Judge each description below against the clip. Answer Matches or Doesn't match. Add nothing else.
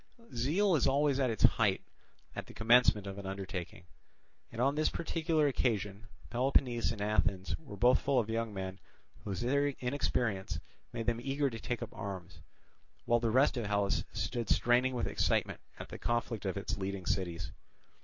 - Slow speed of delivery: Doesn't match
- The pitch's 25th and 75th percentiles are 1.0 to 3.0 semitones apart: Doesn't match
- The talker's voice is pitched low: Matches